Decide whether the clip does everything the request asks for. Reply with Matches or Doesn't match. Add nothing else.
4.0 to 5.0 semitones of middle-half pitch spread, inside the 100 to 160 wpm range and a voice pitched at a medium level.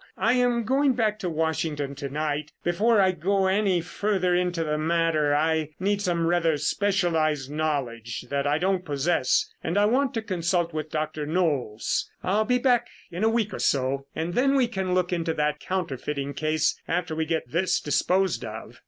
Doesn't match